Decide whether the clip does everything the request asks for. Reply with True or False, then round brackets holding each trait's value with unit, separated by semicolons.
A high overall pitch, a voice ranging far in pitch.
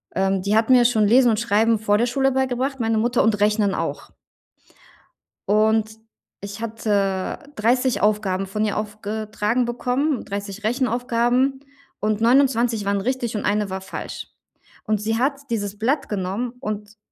False (220 Hz; 2.9 semitones)